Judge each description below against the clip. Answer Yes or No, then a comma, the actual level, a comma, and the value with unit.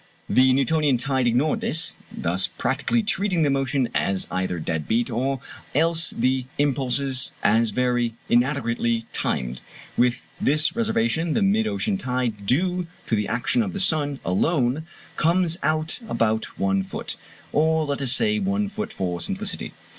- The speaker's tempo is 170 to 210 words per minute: No, average, 150 wpm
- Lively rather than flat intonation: Yes, wide, 5.7 semitones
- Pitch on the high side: No, low, 135 Hz